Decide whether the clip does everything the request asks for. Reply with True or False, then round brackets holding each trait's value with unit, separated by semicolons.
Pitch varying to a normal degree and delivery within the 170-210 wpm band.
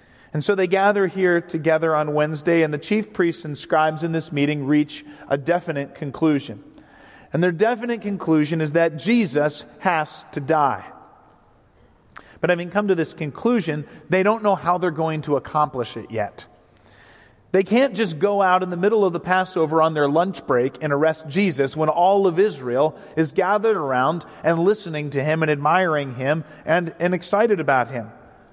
True (4.0 semitones; 175 wpm)